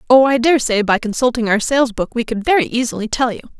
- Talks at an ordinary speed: No, fast, 235 wpm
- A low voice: No, high, 240 Hz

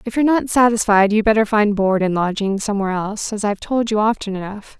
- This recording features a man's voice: No, female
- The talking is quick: Yes, fast, 225 wpm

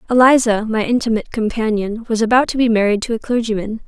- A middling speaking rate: Yes, average, 185 wpm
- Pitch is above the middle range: Yes, high, 225 Hz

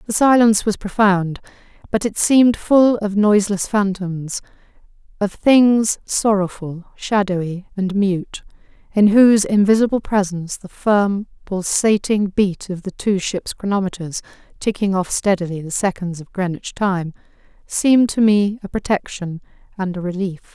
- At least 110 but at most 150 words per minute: Yes, slow, 135 wpm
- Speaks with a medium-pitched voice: No, high, 200 Hz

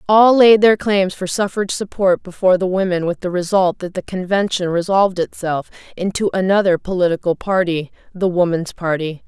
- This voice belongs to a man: No, female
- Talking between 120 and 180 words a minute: Yes, average, 160 wpm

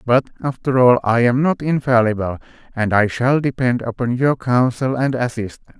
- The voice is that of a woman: No, male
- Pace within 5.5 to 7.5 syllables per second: No, 5.0 syllables/s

